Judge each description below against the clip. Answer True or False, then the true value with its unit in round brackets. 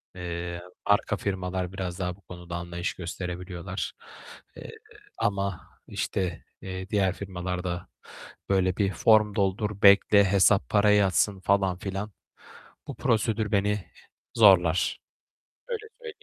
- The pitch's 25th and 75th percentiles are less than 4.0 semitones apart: True (2.4 semitones)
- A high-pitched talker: False (95 Hz)